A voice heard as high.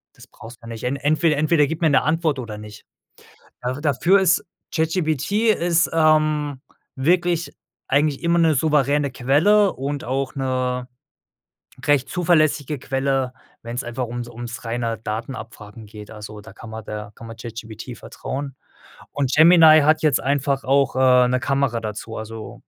No: low, 135 Hz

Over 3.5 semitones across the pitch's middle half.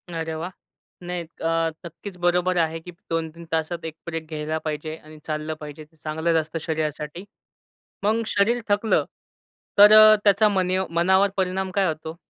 No: average, 3.2 semitones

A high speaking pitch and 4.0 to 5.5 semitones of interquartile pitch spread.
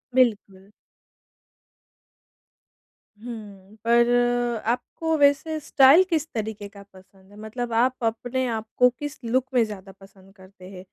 Yes: high, 225 Hz; average, 4.4 semitones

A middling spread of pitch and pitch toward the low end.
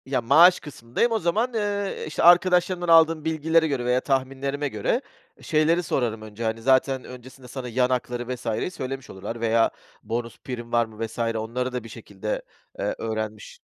No: wide, 5.7 semitones; low, 130 Hz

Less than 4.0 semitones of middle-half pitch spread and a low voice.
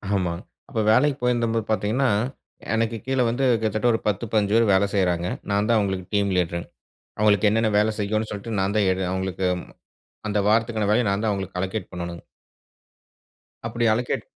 Yes: average, 3.0 semitones; low, 105 Hz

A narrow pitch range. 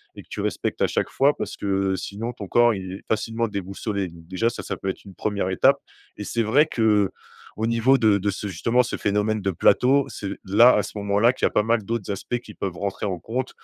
No: average, 3.1 semitones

